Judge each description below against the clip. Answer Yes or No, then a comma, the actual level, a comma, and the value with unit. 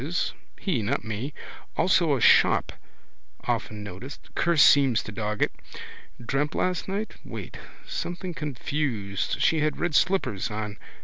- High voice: No, medium, 140 Hz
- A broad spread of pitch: Yes, wide, 8.0 semitones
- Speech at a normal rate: Yes, average, 145 wpm